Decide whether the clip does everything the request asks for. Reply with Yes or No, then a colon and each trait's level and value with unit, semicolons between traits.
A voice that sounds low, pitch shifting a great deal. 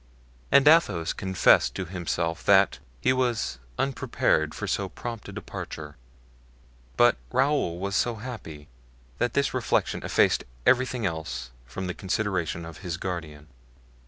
Yes: very low, 95 Hz; wide, 6.8 semitones